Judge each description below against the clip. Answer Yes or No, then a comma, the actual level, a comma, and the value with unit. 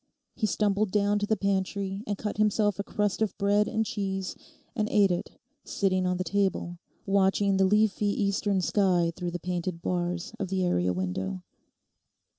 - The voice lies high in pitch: Yes, high, 195 Hz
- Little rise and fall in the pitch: Yes, narrow, 2.3 semitones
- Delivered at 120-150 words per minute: No, average, 170 wpm